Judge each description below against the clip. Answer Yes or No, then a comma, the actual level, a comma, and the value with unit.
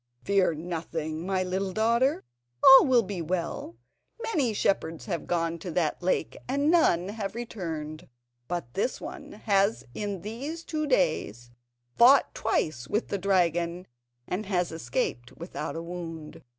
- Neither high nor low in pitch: Yes, medium, 180 Hz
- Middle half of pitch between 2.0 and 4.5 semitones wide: No, average, 4.9 semitones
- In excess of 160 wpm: No, average, 145 wpm